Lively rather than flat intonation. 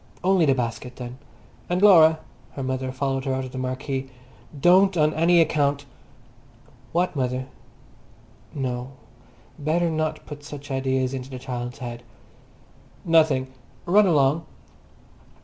No: average, 3.5 semitones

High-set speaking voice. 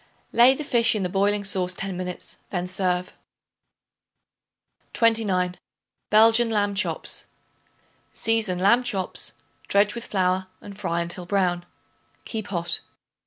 Yes: high, 195 Hz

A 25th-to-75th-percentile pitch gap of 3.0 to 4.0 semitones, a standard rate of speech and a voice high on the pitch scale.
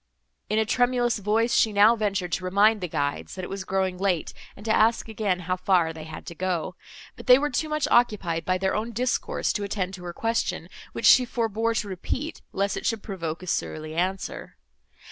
No: average, 3.7 semitones; fast, 210 wpm; high, 200 Hz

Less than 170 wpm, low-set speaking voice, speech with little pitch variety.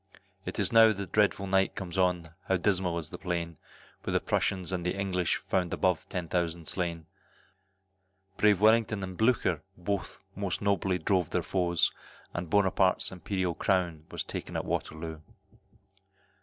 Yes: average, 150 wpm; very low, 90 Hz; narrow, 2.2 semitones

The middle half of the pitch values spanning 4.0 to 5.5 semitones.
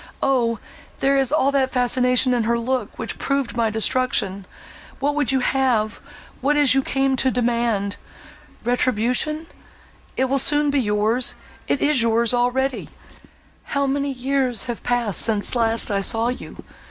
No: average, 2.8 semitones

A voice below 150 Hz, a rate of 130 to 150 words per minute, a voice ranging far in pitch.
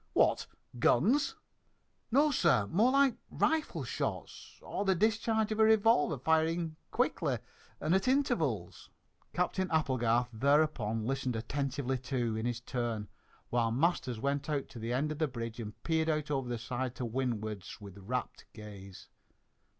Yes: low, 135 Hz; average, 145 wpm; wide, 6.7 semitones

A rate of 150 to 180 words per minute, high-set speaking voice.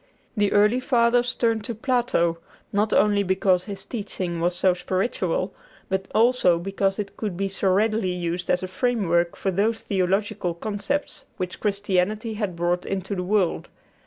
Yes: average, 160 wpm; high, 195 Hz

